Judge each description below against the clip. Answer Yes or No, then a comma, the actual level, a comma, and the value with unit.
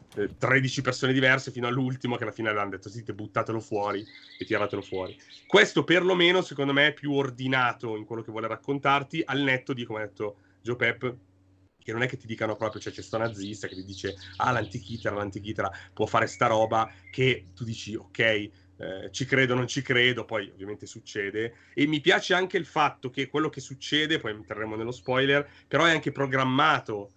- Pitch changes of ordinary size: Yes, average, 4.3 semitones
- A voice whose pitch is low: Yes, low, 115 Hz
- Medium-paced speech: No, fast, 195 wpm